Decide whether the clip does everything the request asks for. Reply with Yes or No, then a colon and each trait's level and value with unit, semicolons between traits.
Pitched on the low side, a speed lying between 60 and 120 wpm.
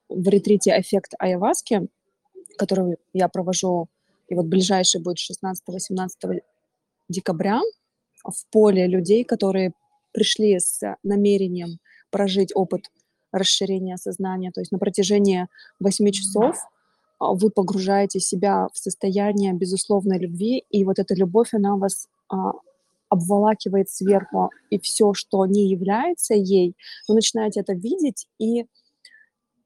No: high, 200 Hz; average, 115 wpm